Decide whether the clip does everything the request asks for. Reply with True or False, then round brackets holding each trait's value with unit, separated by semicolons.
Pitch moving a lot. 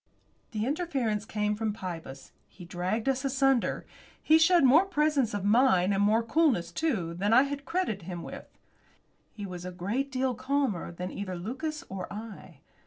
True (6.7 semitones)